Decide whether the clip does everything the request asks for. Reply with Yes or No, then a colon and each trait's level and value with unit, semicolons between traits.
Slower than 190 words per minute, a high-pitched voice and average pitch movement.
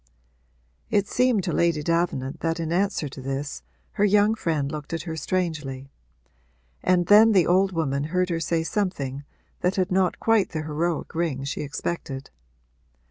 No: average, 160 wpm; medium, 165 Hz; average, 4.1 semitones